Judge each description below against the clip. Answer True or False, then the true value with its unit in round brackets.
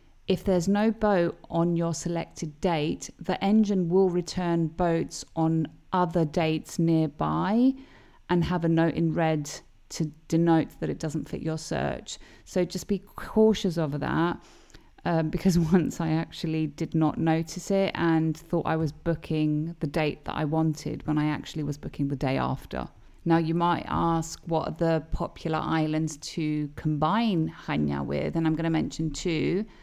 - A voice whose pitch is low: False (165 Hz)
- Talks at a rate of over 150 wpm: True (165 wpm)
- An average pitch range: False (2.2 semitones)